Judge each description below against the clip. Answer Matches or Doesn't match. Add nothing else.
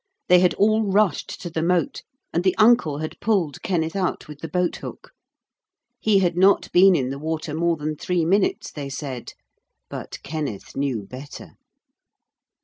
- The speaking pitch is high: Doesn't match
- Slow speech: Doesn't match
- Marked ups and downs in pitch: Doesn't match